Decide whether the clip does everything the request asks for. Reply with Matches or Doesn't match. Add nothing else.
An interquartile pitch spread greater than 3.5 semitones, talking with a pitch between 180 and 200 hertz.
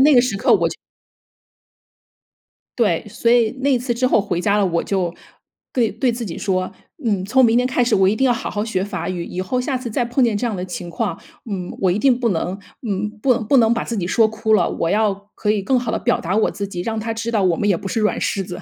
Doesn't match